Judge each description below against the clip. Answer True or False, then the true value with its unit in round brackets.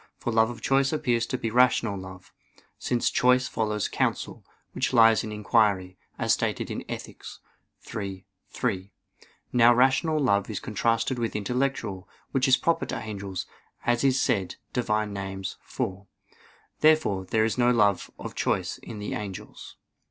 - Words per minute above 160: False (150 wpm)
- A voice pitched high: False (115 Hz)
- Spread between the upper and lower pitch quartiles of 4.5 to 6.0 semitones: False (3.8 semitones)